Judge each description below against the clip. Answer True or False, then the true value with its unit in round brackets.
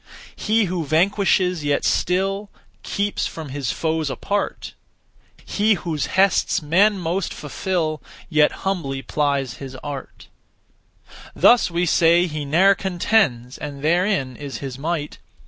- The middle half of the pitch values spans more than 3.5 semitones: True (4.8 semitones)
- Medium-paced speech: False (125 wpm)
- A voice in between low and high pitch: True (165 Hz)